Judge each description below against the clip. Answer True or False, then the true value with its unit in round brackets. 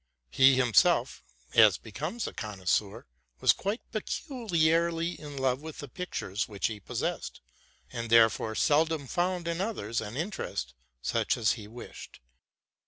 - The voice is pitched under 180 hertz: True (135 Hz)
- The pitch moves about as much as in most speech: False (7.3 semitones)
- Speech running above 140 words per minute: False (135 wpm)